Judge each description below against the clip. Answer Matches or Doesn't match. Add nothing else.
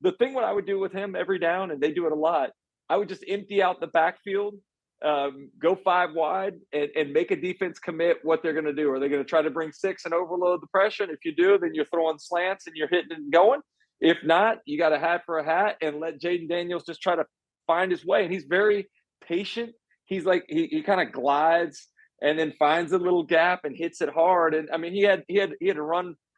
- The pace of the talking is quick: Matches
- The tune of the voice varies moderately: Matches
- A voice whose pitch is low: Doesn't match